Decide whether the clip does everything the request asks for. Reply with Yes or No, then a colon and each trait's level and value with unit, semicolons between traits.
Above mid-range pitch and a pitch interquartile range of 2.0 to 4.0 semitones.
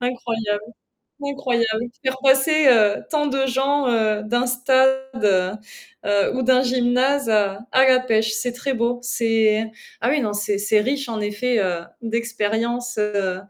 Yes: high, 240 Hz; average, 3.3 semitones